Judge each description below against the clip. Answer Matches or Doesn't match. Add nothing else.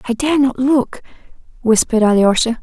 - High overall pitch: Matches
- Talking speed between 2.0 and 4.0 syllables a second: Doesn't match